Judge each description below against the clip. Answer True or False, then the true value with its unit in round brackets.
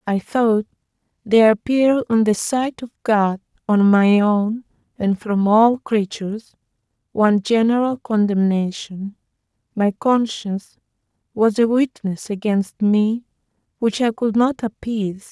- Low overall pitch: False (215 Hz)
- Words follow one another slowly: True (120 wpm)